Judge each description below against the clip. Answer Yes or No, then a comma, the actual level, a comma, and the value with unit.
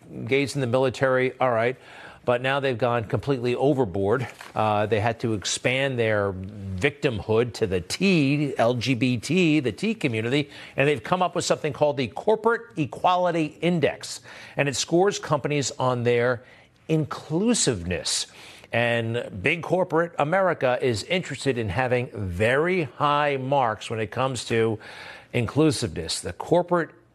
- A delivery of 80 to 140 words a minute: Yes, slow, 135 wpm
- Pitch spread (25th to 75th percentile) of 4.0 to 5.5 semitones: Yes, average, 4.8 semitones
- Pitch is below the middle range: Yes, low, 130 Hz